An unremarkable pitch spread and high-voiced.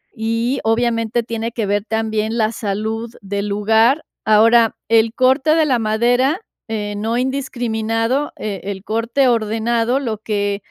No: narrow, 1.9 semitones; high, 225 Hz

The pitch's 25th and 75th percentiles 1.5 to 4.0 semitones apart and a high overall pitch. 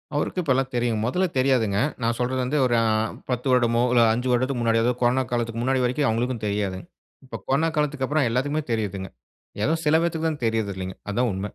No: average, 2.8 semitones; low, 125 Hz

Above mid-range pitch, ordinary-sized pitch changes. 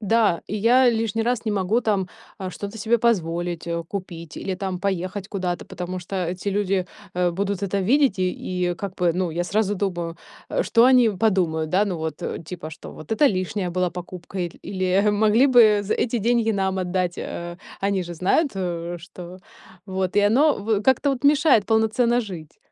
Yes: high, 195 Hz; average, 3.7 semitones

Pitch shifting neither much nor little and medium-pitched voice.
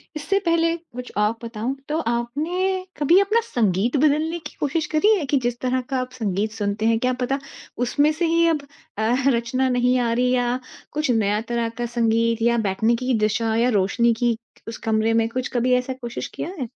No: average, 4.2 semitones; high, 245 Hz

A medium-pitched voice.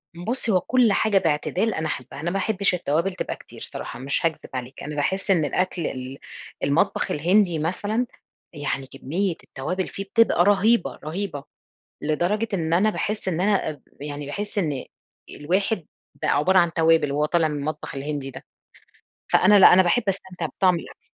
Yes: medium, 175 Hz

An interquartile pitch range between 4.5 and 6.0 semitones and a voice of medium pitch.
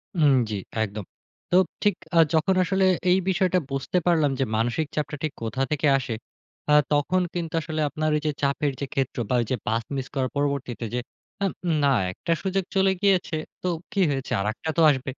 Yes: average, 5.0 semitones; medium, 150 Hz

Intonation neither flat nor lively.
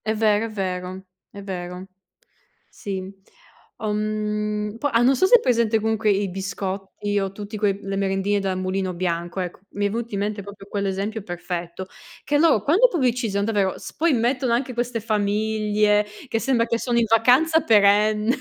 Yes: average, 3.0 semitones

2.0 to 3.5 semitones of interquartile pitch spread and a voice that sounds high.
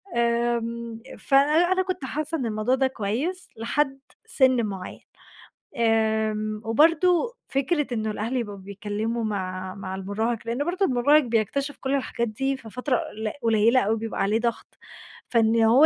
No: average, 3.9 semitones; high, 235 Hz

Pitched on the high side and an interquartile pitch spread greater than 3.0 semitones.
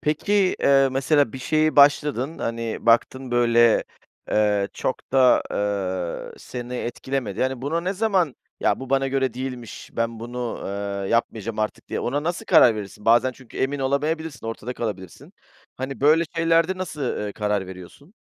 No: low, 130 Hz; average, 3.9 semitones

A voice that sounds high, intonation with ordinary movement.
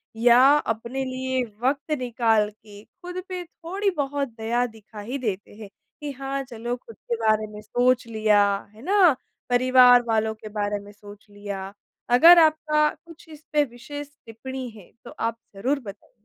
Yes: high, 245 Hz; average, 4.4 semitones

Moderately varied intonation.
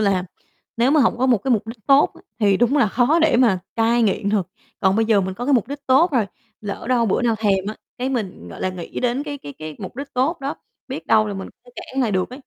Yes: average, 4.8 semitones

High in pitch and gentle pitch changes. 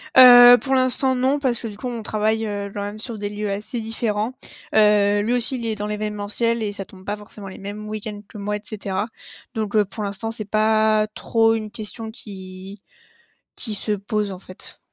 Yes: high, 215 Hz; narrow, 1.8 semitones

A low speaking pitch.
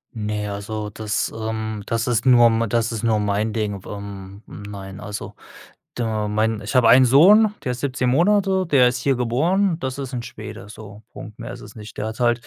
Yes: low, 115 Hz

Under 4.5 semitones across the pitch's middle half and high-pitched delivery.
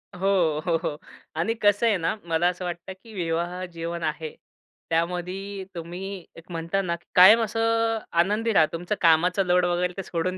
No: average, 2.7 semitones; medium, 180 Hz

